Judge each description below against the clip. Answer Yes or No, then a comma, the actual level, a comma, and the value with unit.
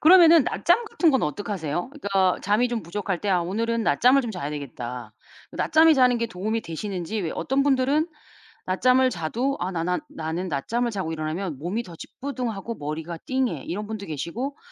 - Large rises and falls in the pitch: Yes, wide, 7.1 semitones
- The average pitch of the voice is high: Yes, high, 205 Hz